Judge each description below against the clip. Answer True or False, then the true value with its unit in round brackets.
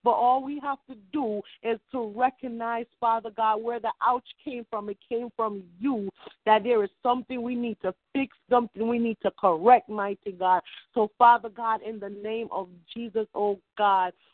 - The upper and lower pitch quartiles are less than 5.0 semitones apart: True (2.9 semitones)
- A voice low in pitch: False (225 Hz)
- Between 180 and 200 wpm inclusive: True (190 wpm)